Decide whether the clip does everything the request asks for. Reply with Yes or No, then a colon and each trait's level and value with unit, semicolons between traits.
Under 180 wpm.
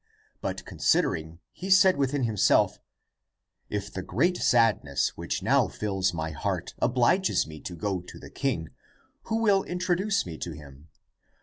Yes: average, 150 wpm